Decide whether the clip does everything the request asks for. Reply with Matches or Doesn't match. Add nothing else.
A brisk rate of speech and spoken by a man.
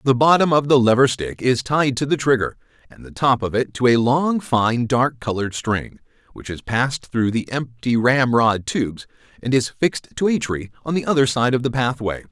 Matches